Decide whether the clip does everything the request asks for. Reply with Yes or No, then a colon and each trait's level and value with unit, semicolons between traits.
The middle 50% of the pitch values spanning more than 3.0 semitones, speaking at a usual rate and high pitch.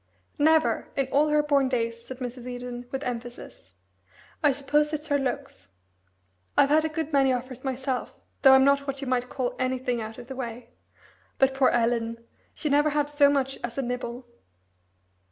No: narrow, 2.5 semitones; average, 175 wpm; very high, 265 Hz